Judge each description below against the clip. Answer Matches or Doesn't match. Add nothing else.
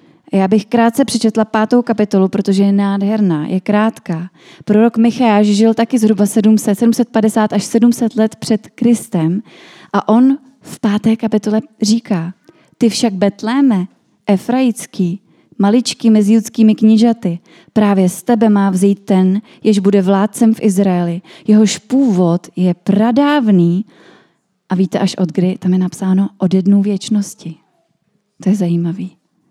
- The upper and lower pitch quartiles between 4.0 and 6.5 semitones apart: Doesn't match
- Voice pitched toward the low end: Doesn't match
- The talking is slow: Doesn't match